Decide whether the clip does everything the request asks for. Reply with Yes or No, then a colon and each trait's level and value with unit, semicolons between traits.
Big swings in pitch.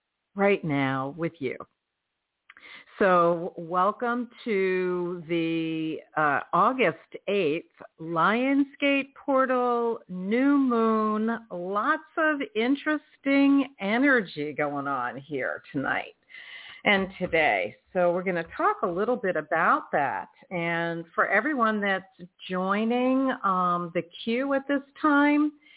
Yes: wide, 7.2 semitones